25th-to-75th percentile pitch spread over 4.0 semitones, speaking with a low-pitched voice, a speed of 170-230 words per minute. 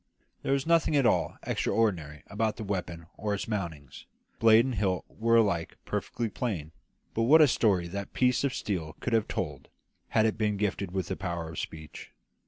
Yes: average, 4.8 semitones; low, 105 Hz; average, 190 wpm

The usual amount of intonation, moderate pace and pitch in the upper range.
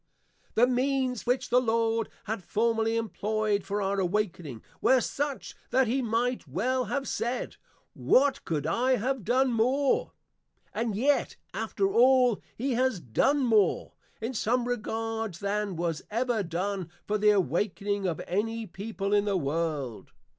Yes: average, 4.1 semitones; average, 145 wpm; high, 225 Hz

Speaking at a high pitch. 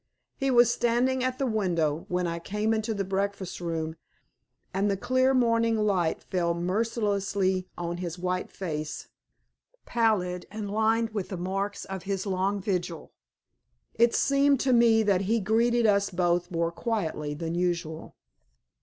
Yes: high, 195 Hz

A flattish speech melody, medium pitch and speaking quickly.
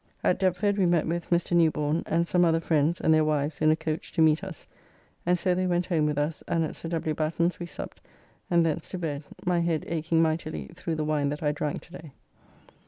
Yes: narrow, 2.0 semitones; medium, 165 Hz; fast, 235 wpm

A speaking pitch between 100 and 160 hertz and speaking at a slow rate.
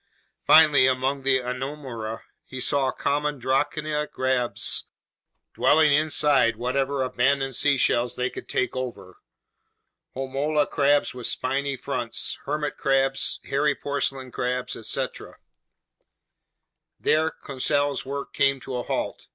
Yes: low, 135 Hz; slow, 110 wpm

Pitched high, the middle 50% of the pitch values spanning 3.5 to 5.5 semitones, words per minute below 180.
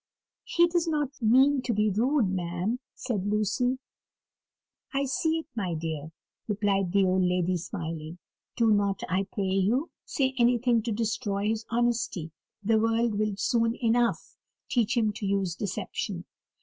Yes: high, 215 Hz; average, 4.1 semitones; average, 150 wpm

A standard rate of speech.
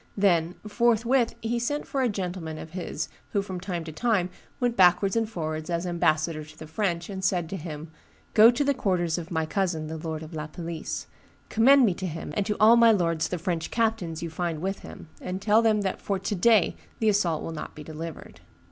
No: fast, 220 wpm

